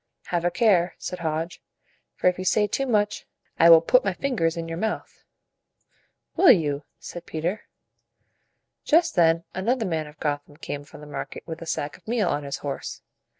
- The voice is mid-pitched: Yes, medium, 170 Hz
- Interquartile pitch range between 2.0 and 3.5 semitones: No, average, 4.9 semitones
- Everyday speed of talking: Yes, average, 185 wpm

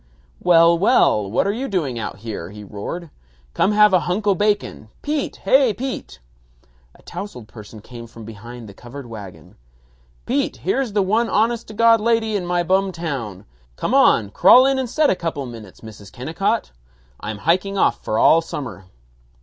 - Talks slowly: No, average, 175 wpm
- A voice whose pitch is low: No, medium, 170 Hz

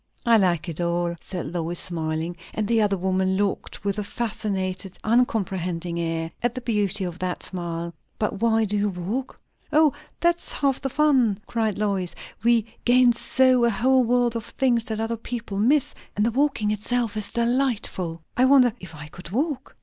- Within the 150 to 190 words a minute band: Yes, average, 180 wpm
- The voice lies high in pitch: Yes, high, 210 Hz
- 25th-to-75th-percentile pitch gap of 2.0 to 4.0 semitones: No, average, 4.9 semitones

